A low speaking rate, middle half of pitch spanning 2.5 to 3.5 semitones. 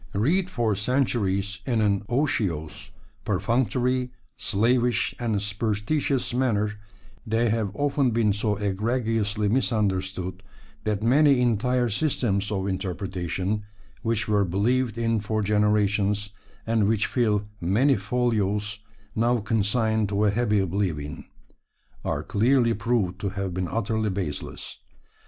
Yes: slow, 115 wpm; average, 3.1 semitones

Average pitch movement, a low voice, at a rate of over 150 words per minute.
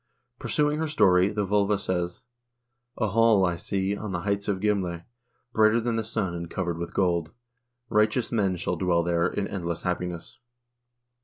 Yes: average, 3.4 semitones; very low, 95 Hz; average, 165 wpm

